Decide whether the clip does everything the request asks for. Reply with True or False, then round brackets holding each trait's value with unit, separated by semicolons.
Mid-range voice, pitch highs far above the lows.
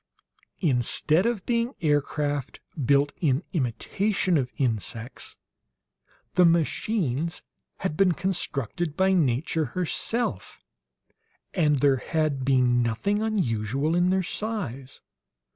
True (155 Hz; 6.0 semitones)